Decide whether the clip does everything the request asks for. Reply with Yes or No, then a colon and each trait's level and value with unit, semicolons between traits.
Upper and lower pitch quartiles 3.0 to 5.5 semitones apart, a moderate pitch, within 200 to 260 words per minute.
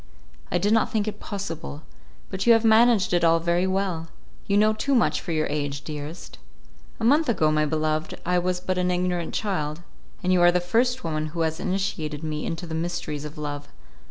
Yes: average, 4.4 semitones; medium, 175 Hz; fast, 205 wpm